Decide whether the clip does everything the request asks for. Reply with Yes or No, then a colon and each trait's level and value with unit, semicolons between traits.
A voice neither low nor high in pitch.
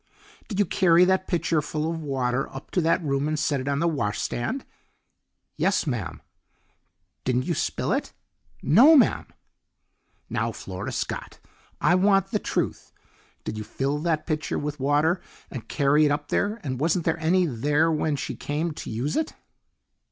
Yes: medium, 155 Hz